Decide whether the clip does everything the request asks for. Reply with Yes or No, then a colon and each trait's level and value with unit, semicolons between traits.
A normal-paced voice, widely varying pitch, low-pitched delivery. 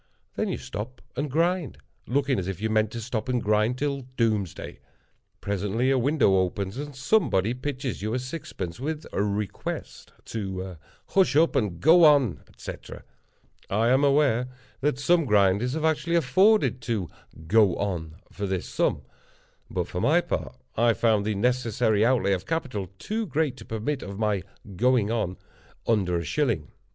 Yes: average, 165 wpm; wide, 5.7 semitones; low, 115 Hz